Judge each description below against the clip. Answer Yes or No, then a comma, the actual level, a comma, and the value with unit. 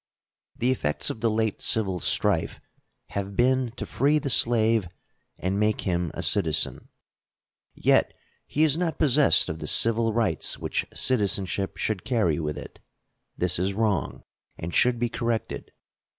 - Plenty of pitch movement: No, average, 4.4 semitones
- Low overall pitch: Yes, low, 110 Hz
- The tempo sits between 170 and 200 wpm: No, average, 150 wpm